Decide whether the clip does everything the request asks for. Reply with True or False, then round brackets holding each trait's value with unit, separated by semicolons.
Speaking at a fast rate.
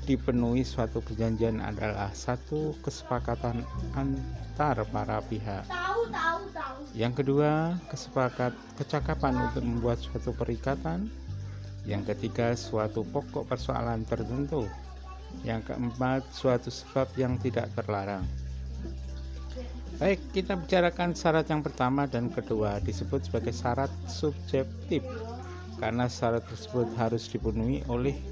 False (100 wpm)